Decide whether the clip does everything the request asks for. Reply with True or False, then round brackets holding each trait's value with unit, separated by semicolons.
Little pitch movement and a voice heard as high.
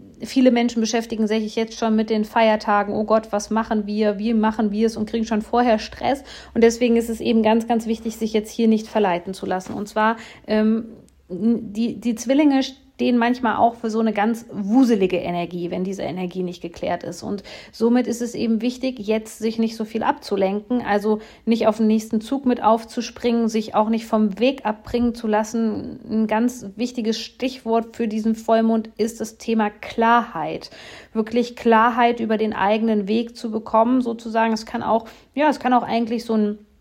True (1.4 semitones; 225 Hz)